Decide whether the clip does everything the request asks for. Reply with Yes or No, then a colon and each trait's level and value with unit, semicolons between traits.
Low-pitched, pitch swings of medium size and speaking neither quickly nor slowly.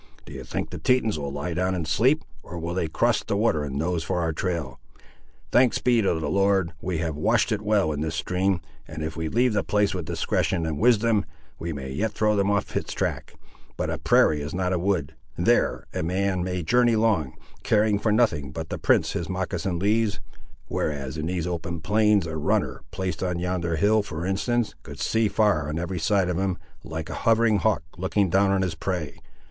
No: very low, 90 Hz; average, 4.5 semitones; fast, 210 wpm